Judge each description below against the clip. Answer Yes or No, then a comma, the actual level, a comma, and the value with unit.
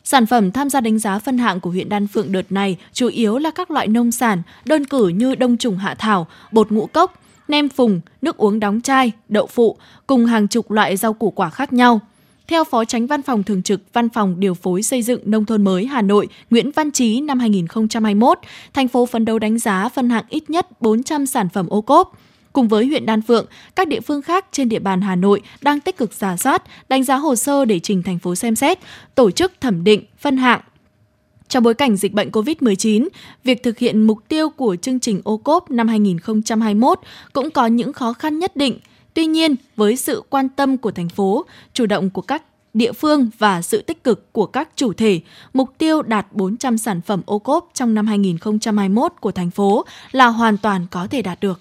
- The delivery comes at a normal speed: Yes, average, 220 wpm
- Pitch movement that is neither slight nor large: Yes, average, 4.3 semitones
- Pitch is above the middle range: Yes, high, 225 Hz